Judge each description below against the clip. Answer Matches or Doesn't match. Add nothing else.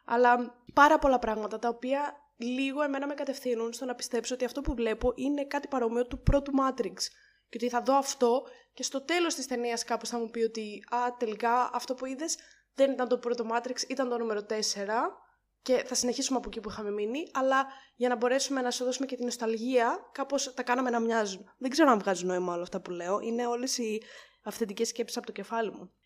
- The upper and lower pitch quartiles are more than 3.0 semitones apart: Doesn't match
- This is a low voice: Doesn't match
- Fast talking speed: Matches